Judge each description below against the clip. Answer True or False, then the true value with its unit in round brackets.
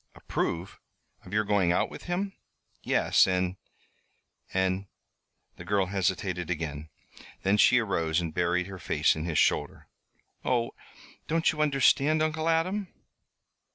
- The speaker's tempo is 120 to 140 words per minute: True (135 wpm)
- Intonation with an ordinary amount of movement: False (8.1 semitones)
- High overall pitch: False (95 Hz)